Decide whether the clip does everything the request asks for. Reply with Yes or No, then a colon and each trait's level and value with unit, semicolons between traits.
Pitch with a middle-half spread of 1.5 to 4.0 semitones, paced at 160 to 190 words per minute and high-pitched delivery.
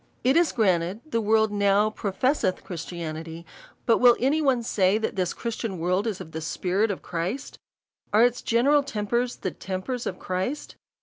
No: average, 4.7 semitones; average, 170 wpm; high, 210 Hz